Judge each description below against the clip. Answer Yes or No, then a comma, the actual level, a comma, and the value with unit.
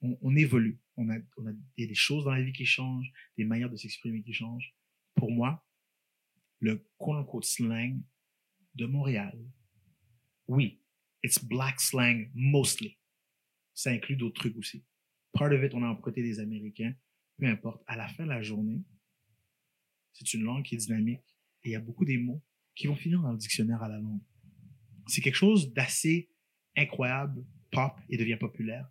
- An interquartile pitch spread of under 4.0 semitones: Yes, average, 3.4 semitones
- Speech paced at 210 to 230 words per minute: No, average, 170 wpm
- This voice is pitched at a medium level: No, low, 120 Hz